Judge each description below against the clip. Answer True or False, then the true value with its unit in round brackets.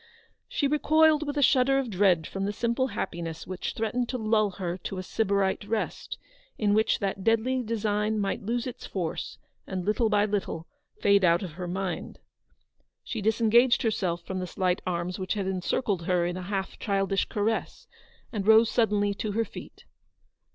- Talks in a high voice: True (205 Hz)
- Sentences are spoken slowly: False (175 wpm)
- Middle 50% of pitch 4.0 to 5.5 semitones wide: False (3.4 semitones)